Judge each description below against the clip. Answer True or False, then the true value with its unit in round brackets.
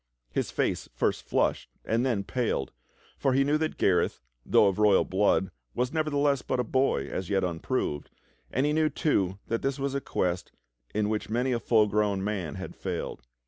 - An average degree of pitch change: False (5.8 semitones)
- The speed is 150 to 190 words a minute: True (185 wpm)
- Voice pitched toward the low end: True (115 Hz)